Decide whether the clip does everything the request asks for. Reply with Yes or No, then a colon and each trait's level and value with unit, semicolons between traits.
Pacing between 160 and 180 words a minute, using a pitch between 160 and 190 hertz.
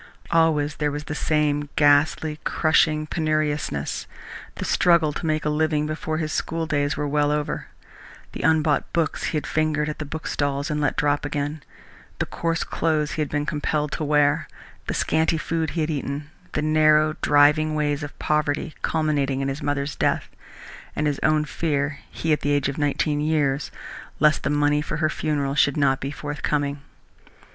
No: average, 175 wpm; medium, 150 Hz